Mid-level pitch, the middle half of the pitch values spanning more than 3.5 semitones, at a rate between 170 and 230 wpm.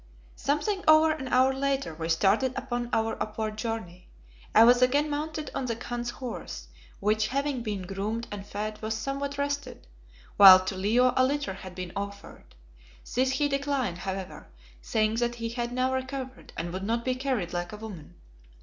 No: high, 240 Hz; average, 4.8 semitones; average, 175 wpm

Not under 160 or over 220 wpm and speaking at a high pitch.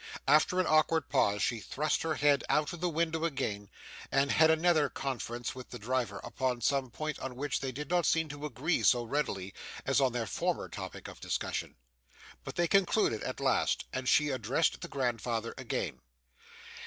No: average, 185 wpm; medium, 140 Hz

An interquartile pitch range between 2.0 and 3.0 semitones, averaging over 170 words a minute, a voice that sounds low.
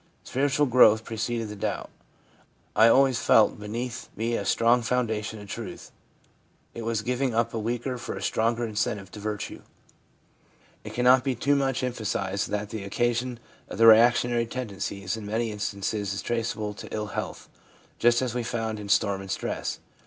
No: narrow, 2.4 semitones; average, 165 wpm; low, 115 Hz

